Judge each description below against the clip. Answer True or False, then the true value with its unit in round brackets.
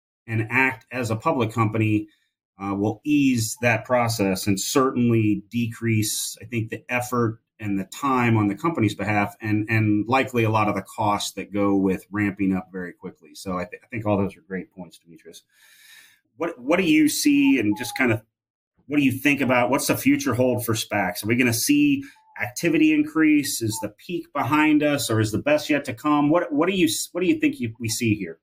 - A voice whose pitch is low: True (115 Hz)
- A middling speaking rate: False (215 wpm)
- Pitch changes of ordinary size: False (5.8 semitones)